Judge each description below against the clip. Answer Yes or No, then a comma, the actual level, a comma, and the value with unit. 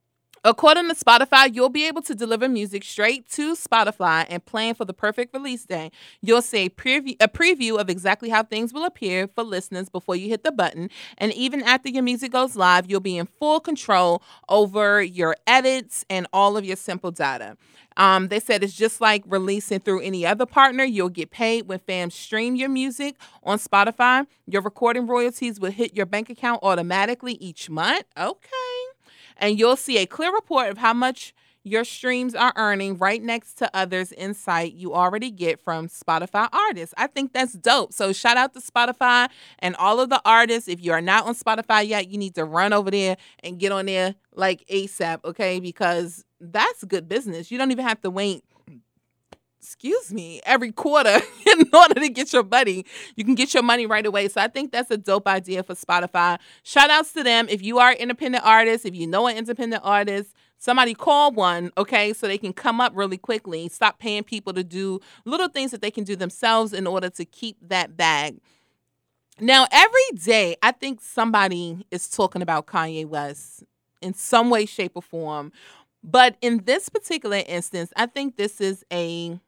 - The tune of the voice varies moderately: Yes, average, 4.9 semitones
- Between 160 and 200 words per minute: Yes, average, 195 wpm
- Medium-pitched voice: No, high, 215 Hz